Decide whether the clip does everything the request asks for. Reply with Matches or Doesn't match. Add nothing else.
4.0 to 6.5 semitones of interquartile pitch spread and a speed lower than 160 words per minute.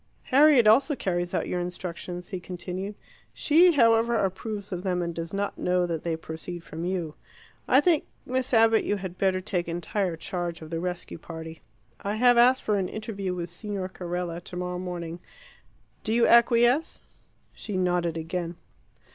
Doesn't match